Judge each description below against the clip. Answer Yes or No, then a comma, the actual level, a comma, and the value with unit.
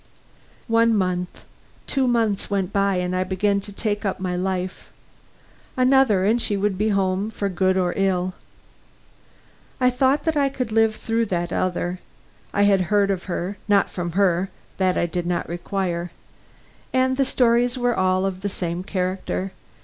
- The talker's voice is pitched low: No, high, 195 Hz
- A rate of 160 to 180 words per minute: Yes, average, 165 wpm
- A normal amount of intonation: Yes, average, 3.4 semitones